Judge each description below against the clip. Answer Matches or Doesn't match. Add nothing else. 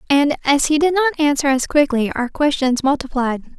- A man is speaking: Doesn't match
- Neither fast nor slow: Matches